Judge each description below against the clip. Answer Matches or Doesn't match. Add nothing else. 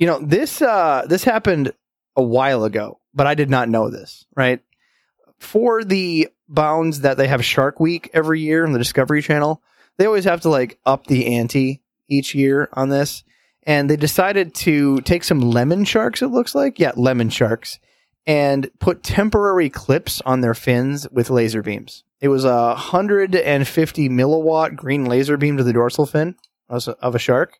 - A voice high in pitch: Doesn't match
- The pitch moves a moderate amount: Matches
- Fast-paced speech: Doesn't match